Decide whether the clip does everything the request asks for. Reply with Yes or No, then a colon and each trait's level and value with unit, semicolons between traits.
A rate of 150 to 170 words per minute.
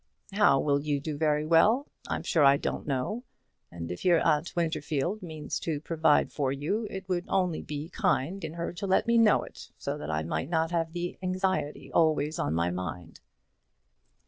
No: average, 190 wpm